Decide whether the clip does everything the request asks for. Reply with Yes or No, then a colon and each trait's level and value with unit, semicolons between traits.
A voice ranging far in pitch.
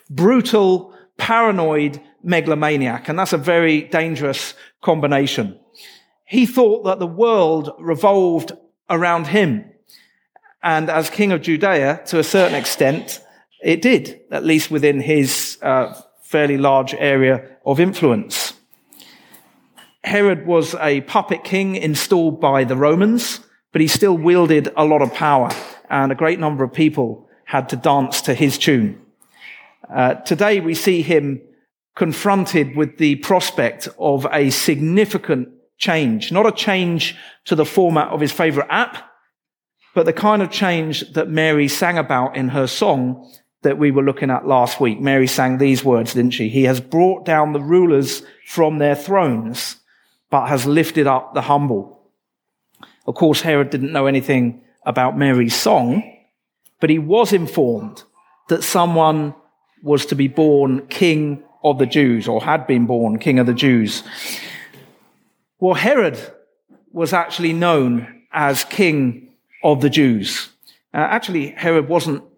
No: average, 4.2 semitones